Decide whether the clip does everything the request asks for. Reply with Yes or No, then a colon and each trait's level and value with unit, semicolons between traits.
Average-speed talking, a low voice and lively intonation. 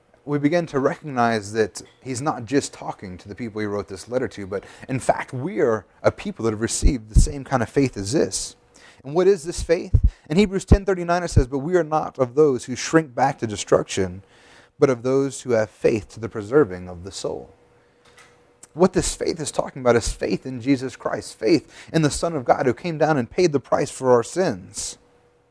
No: fast, 220 wpm; low, 130 Hz; wide, 6.2 semitones